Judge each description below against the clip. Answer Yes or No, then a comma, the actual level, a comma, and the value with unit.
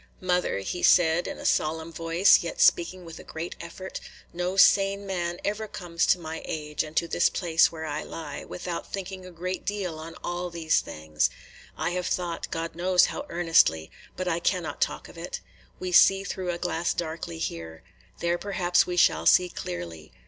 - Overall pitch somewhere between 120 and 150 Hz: No, medium, 170 Hz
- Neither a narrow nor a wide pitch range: No, narrow, 2.1 semitones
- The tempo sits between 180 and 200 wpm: Yes, average, 190 wpm